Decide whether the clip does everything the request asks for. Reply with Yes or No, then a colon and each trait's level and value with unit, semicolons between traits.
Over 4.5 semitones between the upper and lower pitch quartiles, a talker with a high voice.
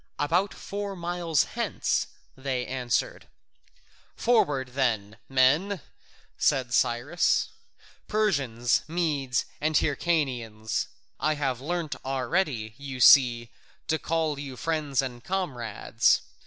No: average, 4.9 semitones; medium, 140 Hz